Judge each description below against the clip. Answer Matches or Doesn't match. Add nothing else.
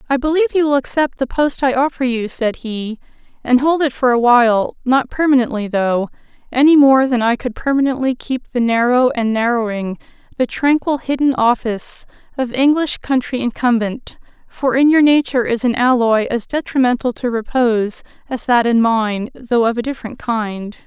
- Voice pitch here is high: Matches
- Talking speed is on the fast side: Doesn't match